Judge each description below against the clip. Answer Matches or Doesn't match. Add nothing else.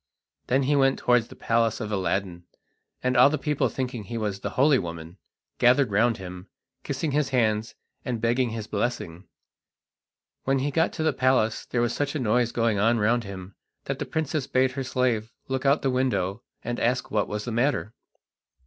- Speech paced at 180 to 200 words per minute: Matches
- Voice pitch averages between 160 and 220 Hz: Doesn't match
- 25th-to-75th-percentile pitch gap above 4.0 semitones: Doesn't match